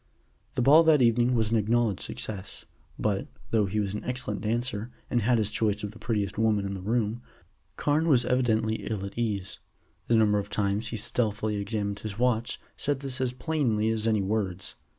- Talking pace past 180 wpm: Yes, average, 190 wpm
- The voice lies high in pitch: No, low, 110 Hz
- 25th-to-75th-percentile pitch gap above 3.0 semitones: No, average, 2.7 semitones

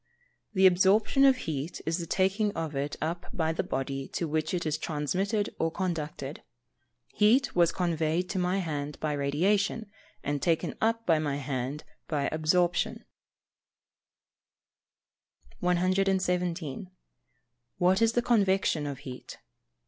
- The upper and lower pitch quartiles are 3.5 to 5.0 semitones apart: Yes, average, 4.2 semitones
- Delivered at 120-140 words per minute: Yes, slow, 135 wpm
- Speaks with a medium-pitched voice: Yes, medium, 170 Hz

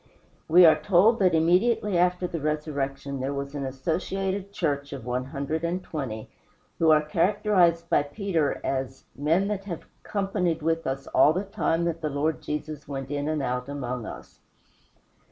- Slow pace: No, average, 170 wpm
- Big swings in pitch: No, average, 4.3 semitones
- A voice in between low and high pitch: Yes, medium, 155 Hz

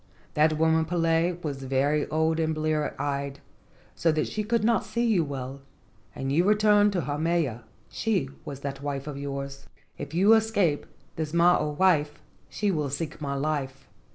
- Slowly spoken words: No, average, 170 wpm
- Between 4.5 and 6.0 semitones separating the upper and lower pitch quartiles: No, average, 3.9 semitones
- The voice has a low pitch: No, medium, 155 Hz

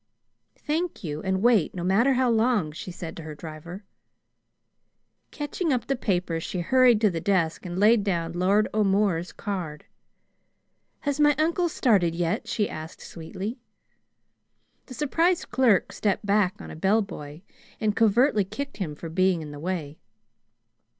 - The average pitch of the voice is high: Yes, high, 195 Hz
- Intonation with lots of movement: Yes, wide, 5.9 semitones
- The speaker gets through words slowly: No, average, 150 wpm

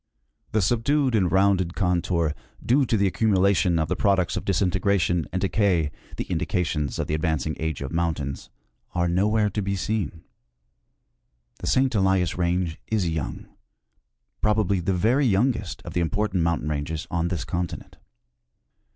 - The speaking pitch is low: Yes, very low, 90 Hz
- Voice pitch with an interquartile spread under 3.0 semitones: No, average, 3.6 semitones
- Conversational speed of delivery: Yes, average, 150 wpm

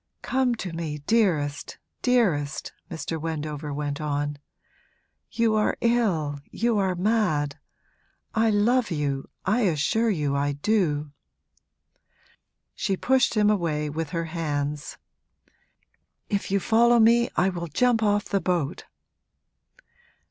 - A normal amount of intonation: No, wide, 6.8 semitones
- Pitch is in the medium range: Yes, medium, 175 Hz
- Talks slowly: Yes, slow, 120 wpm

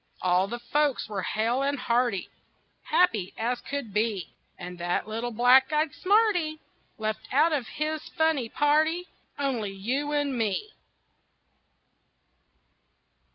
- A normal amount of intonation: No, wide, 5.8 semitones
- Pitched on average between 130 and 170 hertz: No, very high, 250 Hz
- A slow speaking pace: Yes, slow, 120 wpm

